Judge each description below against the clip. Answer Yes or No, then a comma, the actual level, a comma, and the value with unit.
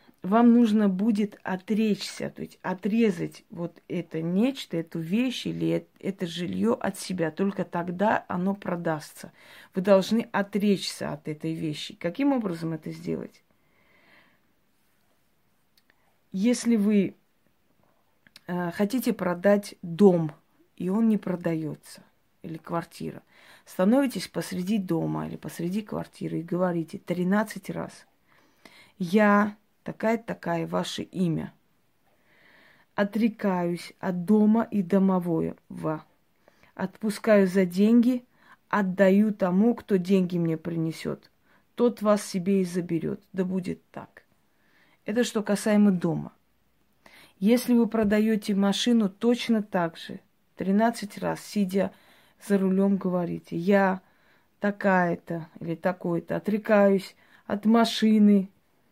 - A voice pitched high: Yes, high, 195 Hz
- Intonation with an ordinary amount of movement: Yes, average, 3.6 semitones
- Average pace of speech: No, slow, 105 wpm